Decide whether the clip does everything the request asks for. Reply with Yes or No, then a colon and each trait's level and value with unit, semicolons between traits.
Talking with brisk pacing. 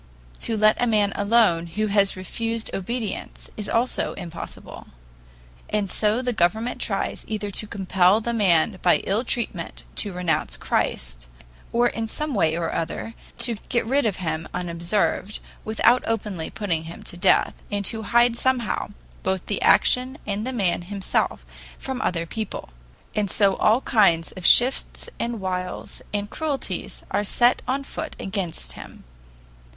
No: average, 155 wpm